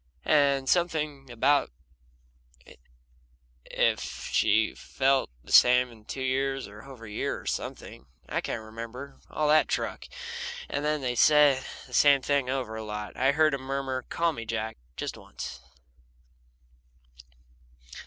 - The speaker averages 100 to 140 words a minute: Yes, slow, 135 wpm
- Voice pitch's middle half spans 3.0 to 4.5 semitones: Yes, average, 3.6 semitones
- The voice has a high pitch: No, low, 135 Hz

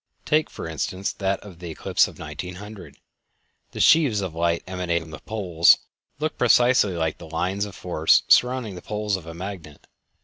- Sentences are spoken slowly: No, average, 175 wpm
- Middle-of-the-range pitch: No, very low, 95 Hz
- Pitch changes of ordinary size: Yes, average, 3.8 semitones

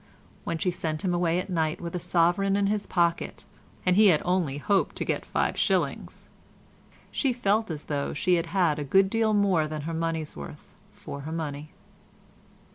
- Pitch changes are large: No, average, 3.8 semitones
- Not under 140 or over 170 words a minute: No, average, 190 wpm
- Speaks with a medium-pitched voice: Yes, medium, 170 Hz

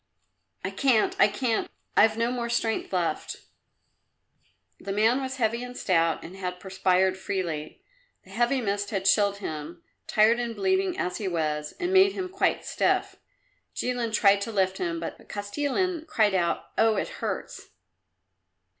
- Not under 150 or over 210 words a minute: Yes, average, 155 wpm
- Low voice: No, high, 210 Hz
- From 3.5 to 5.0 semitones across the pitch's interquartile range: Yes, average, 4.6 semitones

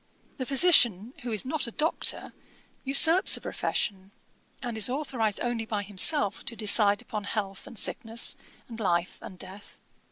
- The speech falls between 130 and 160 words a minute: Yes, average, 155 wpm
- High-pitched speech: Yes, high, 225 Hz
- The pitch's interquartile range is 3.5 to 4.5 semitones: Yes, average, 4.1 semitones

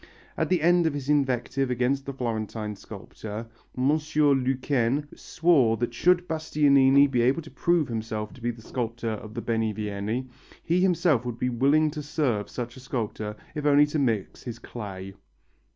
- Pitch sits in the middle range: No, low, 130 Hz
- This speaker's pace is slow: No, average, 170 wpm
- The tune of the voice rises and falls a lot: No, average, 4.5 semitones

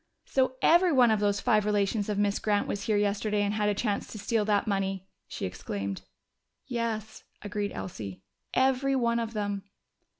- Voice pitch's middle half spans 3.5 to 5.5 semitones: No, narrow, 2.5 semitones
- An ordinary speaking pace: Yes, average, 175 wpm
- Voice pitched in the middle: No, high, 210 Hz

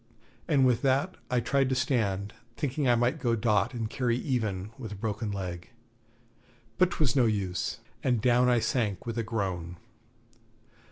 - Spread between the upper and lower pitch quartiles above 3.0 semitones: Yes, average, 3.8 semitones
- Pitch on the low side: Yes, low, 115 Hz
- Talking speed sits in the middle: Yes, average, 165 wpm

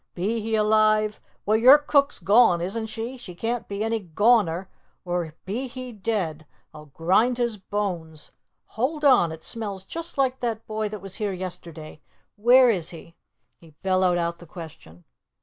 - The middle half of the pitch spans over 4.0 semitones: Yes, average, 5.0 semitones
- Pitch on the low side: No, high, 210 Hz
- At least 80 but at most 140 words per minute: No, average, 165 wpm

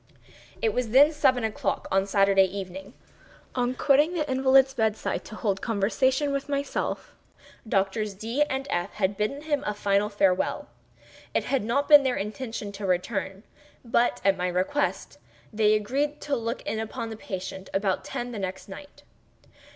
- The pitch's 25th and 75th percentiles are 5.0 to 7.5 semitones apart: Yes, average, 5.3 semitones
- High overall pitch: Yes, high, 220 Hz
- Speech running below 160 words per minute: No, average, 165 wpm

